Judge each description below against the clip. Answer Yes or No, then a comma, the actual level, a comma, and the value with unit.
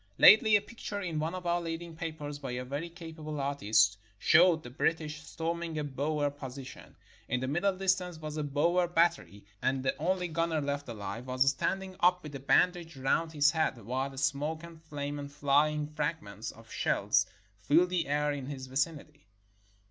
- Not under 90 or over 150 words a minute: No, average, 180 wpm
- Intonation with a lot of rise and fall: No, average, 3.3 semitones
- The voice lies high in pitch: No, medium, 150 Hz